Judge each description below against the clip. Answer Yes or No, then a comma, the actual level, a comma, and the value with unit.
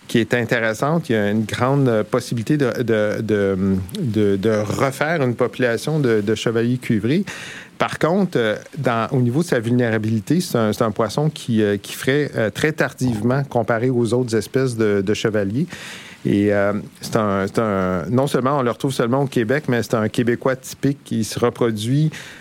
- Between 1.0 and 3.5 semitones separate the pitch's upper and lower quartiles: No, average, 3.9 semitones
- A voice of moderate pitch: No, low, 120 Hz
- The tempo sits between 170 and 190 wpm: Yes, average, 180 wpm